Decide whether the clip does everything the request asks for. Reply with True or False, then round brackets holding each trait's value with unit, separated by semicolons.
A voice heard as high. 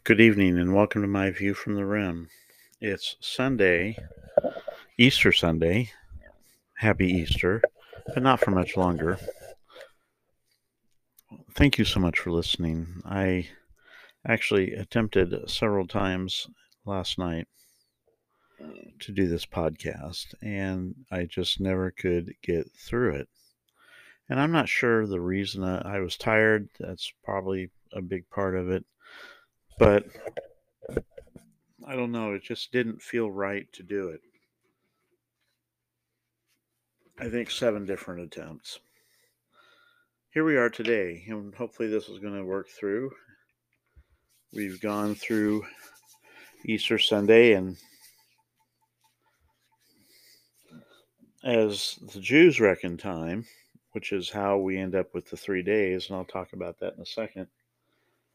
False (100 Hz)